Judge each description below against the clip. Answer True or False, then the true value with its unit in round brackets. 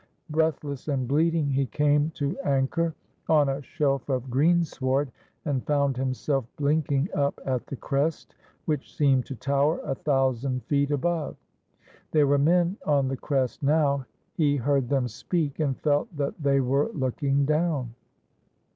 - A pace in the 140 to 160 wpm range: True (150 wpm)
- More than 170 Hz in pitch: False (140 Hz)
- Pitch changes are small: True (2.1 semitones)